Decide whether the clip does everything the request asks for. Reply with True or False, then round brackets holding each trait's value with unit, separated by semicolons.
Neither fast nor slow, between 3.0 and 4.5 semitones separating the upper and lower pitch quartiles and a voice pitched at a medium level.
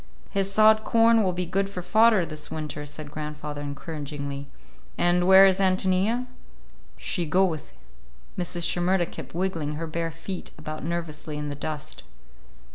True (150 wpm; 4.0 semitones; 170 Hz)